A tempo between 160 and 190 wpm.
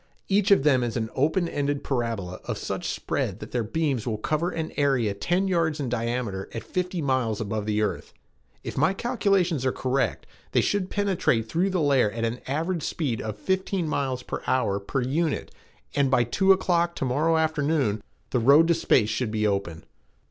Yes: average, 185 wpm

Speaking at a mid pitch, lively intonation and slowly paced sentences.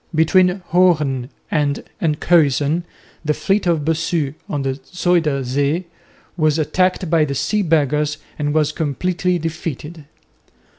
No: medium, 155 Hz; average, 3.2 semitones; slow, 120 wpm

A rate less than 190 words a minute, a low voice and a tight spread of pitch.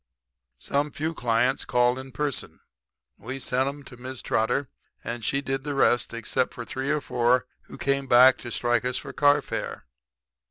Yes: average, 170 wpm; low, 130 Hz; narrow, 2.3 semitones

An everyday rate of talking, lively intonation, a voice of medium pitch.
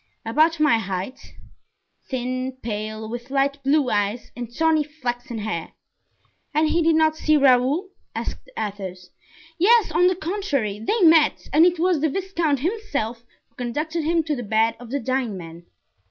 No: average, 160 wpm; wide, 5.9 semitones; very high, 270 Hz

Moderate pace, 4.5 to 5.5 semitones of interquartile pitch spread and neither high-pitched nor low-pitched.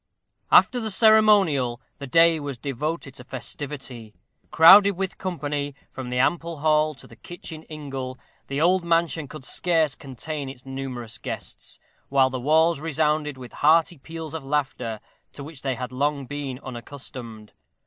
No: average, 150 wpm; average, 3.7 semitones; medium, 145 Hz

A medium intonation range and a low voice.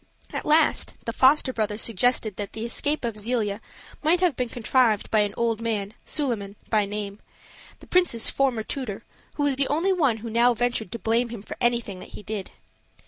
No: average, 3.5 semitones; high, 230 Hz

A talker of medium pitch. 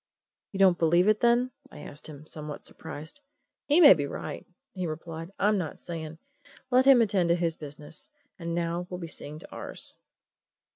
Yes: medium, 170 Hz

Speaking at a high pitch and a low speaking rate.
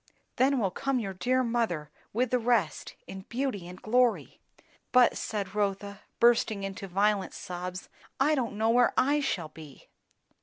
No: high, 215 Hz; average, 160 wpm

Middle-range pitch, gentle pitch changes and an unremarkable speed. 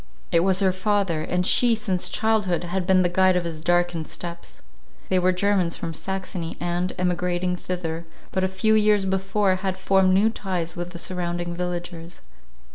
Yes: medium, 180 Hz; narrow, 1.7 semitones; average, 175 wpm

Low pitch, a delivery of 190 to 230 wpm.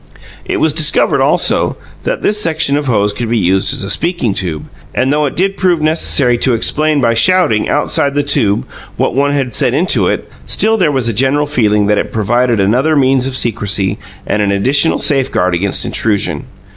Yes: low, 130 Hz; average, 195 wpm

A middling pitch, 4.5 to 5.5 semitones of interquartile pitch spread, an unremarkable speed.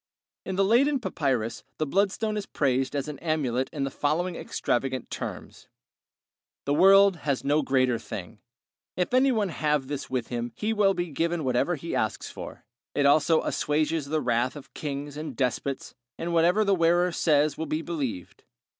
Yes: medium, 150 Hz; average, 4.8 semitones; average, 170 wpm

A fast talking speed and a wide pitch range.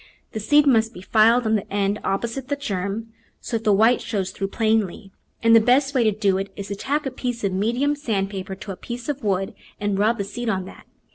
No: fast, 240 wpm; average, 3.5 semitones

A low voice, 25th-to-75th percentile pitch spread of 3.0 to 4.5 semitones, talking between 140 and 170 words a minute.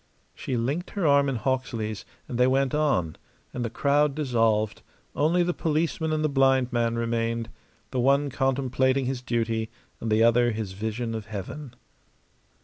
Yes: low, 125 Hz; average, 3.5 semitones; average, 160 wpm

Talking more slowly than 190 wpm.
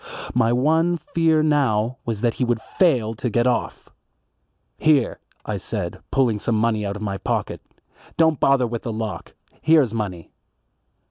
Yes: average, 155 wpm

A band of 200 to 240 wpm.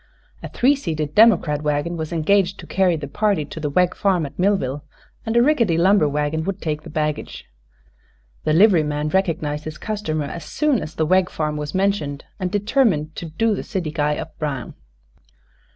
No: average, 185 wpm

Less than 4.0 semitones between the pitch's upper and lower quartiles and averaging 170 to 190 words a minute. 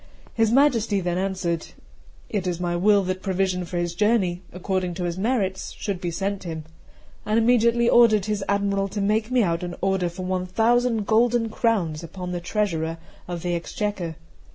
Yes: average, 3.5 semitones; average, 175 wpm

